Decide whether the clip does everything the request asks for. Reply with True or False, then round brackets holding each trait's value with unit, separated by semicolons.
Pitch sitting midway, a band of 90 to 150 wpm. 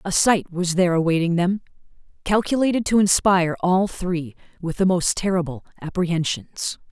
True (180 Hz; 140 wpm)